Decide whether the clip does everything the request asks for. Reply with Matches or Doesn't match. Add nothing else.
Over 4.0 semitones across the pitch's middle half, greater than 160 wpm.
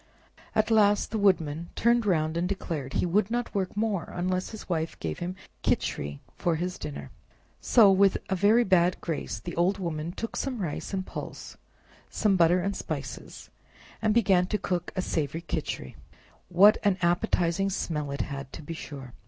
Doesn't match